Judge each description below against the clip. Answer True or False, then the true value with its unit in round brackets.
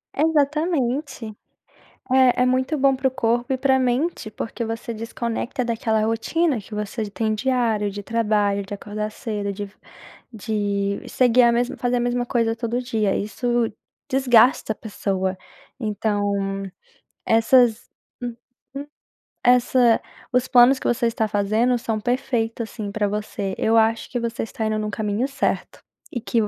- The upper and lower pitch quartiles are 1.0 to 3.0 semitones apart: True (2.7 semitones)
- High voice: True (230 Hz)